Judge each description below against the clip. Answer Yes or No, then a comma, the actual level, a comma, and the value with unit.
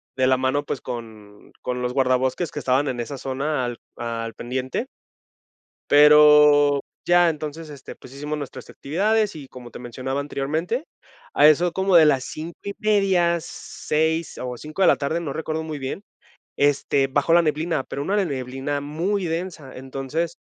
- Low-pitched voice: No, medium, 145 Hz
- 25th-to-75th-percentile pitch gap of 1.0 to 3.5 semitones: No, average, 4.0 semitones